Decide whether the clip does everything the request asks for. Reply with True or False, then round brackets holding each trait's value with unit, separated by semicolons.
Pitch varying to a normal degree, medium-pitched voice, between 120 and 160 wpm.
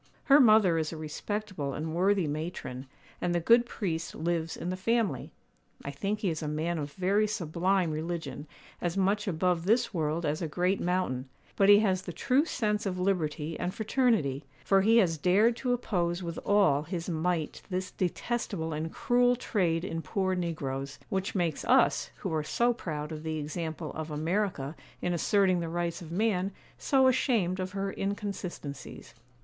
False (4.1 semitones; 180 Hz; 175 wpm)